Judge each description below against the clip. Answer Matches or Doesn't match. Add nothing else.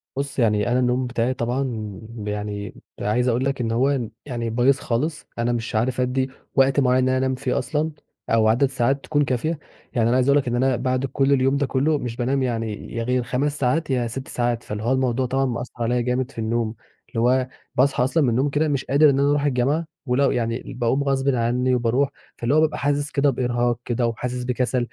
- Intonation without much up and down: Matches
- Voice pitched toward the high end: Doesn't match